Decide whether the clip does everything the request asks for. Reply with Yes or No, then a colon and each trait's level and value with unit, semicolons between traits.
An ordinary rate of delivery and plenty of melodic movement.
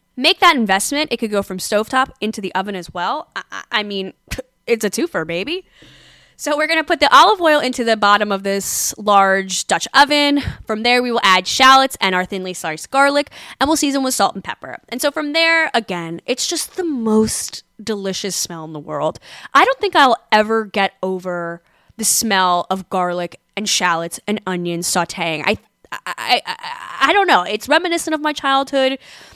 Yes: average, 190 wpm; wide, 7.2 semitones